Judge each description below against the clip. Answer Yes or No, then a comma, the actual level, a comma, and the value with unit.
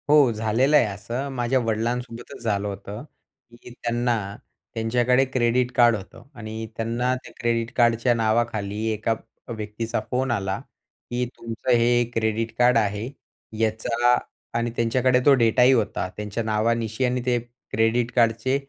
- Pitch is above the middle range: No, low, 115 Hz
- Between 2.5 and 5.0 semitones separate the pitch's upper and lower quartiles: No, narrow, 1.8 semitones